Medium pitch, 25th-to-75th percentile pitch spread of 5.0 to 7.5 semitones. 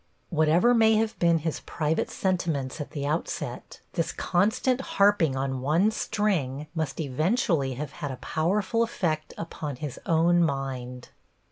Yes: medium, 160 Hz; average, 5.3 semitones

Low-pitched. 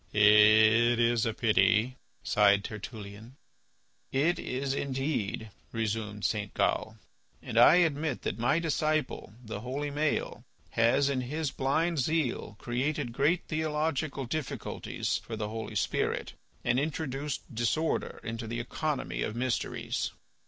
Yes: low, 125 Hz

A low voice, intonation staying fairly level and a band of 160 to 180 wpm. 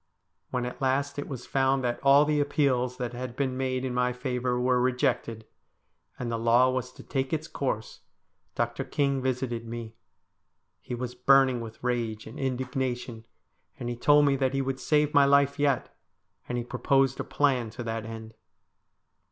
Yes: low, 125 Hz; narrow, 2.1 semitones; average, 175 wpm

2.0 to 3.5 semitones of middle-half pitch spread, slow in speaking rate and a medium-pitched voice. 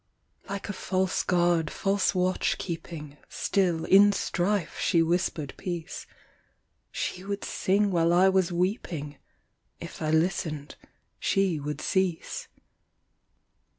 Yes: average, 2.9 semitones; slow, 115 wpm; medium, 180 Hz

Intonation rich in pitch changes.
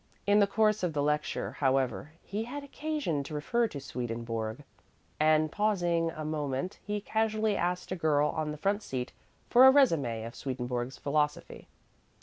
Yes: wide, 7.1 semitones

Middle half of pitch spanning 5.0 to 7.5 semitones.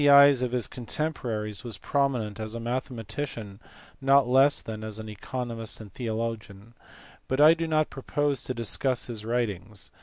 No: average, 3.9 semitones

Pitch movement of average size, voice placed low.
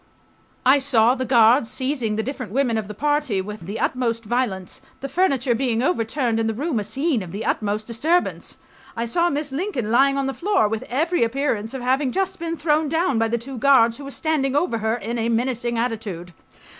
No: average, 4.0 semitones; very high, 250 Hz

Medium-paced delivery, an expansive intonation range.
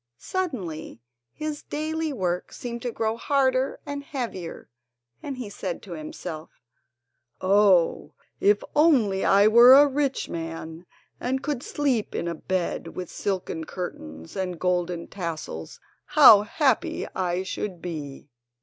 No: slow, 130 wpm; wide, 7.3 semitones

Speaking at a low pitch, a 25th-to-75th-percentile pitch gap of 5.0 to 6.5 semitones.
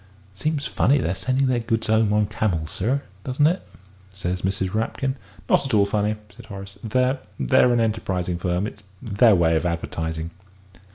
Yes: low, 105 Hz; wide, 5.4 semitones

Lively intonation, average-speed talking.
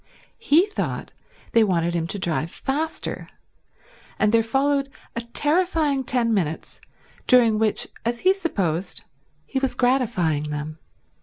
No: wide, 8.1 semitones; slow, 130 wpm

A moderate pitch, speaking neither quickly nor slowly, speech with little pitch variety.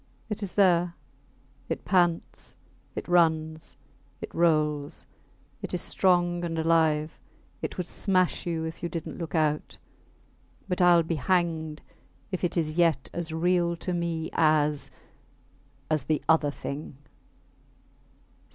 No: medium, 165 Hz; slow, 130 wpm; narrow, 1.9 semitones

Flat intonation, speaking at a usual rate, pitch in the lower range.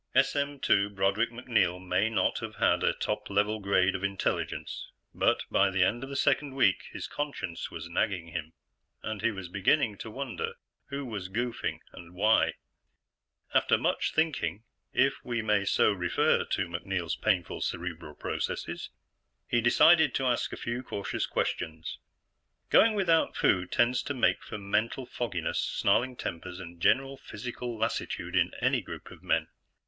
No: wide, 5.4 semitones; average, 155 wpm; low, 105 Hz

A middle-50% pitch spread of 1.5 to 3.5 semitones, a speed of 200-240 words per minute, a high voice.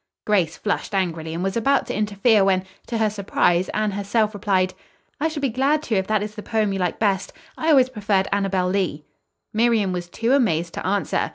Yes: average, 2.9 semitones; fast, 205 wpm; high, 205 Hz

